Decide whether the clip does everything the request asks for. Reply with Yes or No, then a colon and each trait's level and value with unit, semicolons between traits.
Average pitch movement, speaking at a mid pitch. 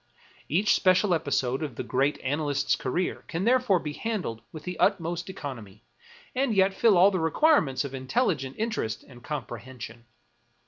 No: wide, 6.7 semitones; medium, 155 Hz